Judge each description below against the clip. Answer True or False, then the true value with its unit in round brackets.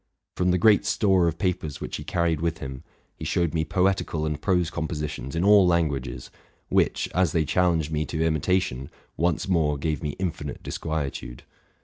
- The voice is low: True (80 Hz)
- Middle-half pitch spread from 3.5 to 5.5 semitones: False (3.1 semitones)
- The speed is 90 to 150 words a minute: False (170 wpm)